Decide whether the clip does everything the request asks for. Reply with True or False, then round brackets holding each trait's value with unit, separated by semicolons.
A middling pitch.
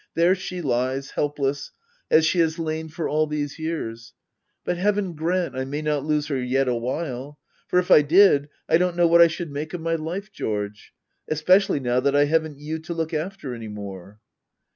True (155 Hz)